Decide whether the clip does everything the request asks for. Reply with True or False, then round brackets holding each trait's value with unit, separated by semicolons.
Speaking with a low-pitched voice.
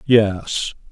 True (105 Hz)